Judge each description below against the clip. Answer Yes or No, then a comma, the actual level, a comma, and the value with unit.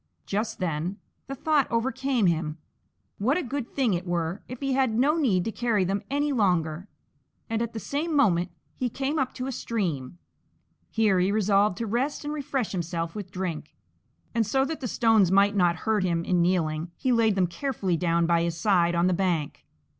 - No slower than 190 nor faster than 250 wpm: Yes, average, 195 wpm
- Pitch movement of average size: No, wide, 6.5 semitones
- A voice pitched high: Yes, high, 205 Hz